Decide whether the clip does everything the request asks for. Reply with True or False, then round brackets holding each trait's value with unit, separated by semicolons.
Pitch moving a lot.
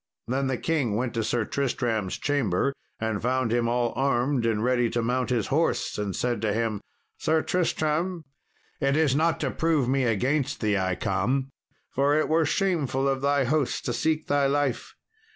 False (3.8 semitones)